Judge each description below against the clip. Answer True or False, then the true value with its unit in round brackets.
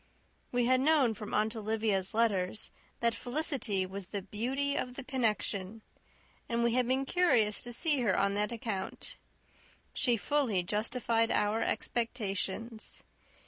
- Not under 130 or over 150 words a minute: True (140 wpm)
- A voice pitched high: True (230 Hz)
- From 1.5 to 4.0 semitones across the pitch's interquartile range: True (3.3 semitones)